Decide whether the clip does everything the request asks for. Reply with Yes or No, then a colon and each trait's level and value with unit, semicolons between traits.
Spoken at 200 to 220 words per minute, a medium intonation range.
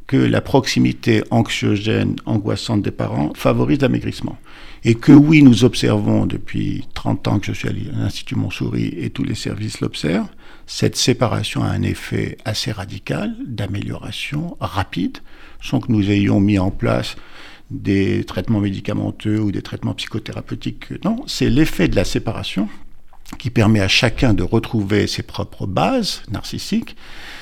No: slow, 145 wpm; average, 3.7 semitones